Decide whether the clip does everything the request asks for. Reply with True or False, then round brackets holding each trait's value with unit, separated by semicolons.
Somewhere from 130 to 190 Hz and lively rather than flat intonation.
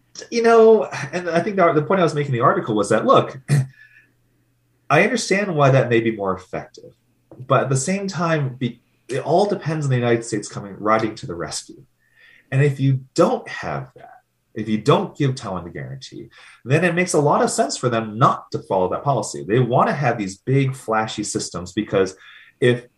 True (135 Hz; 6.8 semitones)